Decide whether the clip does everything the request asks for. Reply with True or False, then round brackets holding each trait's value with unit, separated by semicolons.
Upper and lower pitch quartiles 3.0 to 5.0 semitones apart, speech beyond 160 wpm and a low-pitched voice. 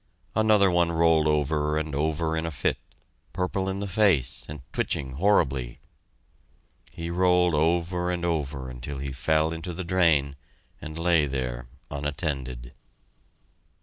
False (4.0 semitones; 135 wpm; 80 Hz)